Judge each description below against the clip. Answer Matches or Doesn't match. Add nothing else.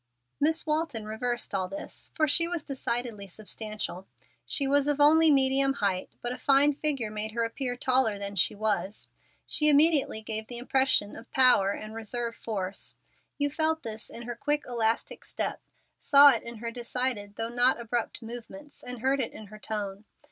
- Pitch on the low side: Doesn't match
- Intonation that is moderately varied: Matches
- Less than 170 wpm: Doesn't match